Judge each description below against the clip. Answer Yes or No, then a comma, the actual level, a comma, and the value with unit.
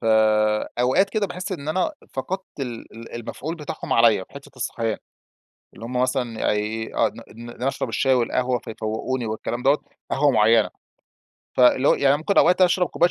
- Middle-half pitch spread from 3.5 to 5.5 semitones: Yes, average, 4.8 semitones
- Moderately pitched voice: No, low, 130 Hz